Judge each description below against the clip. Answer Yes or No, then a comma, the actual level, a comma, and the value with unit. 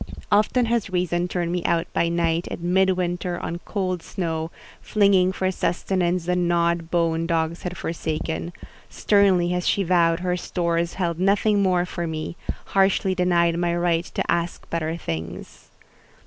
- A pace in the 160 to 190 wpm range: No, average, 150 wpm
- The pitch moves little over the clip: Yes, narrow, 1.6 semitones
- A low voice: No, medium, 175 Hz